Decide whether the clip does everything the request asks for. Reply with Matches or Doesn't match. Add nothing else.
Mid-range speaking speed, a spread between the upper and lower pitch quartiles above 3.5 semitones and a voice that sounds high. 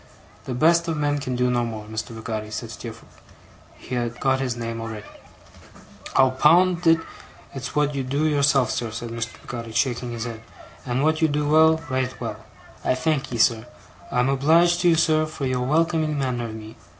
Doesn't match